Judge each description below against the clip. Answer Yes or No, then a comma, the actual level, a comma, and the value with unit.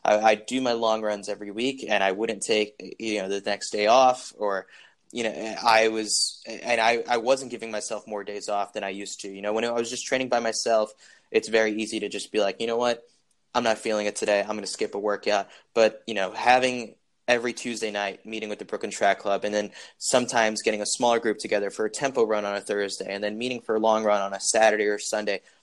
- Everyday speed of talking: No, fast, 245 wpm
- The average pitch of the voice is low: Yes, low, 110 Hz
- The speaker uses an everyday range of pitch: No, narrow, 2.1 semitones